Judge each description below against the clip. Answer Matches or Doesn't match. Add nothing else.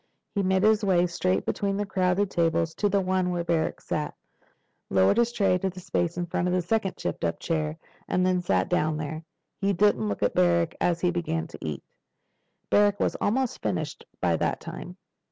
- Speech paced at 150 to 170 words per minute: Doesn't match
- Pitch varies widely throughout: Doesn't match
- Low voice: Doesn't match